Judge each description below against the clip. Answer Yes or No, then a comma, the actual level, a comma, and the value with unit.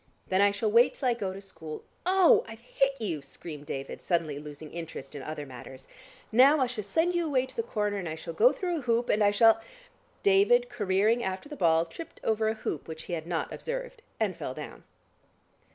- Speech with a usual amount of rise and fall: No, wide, 8.1 semitones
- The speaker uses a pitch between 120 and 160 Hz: No, high, 210 Hz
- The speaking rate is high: Yes, fast, 220 wpm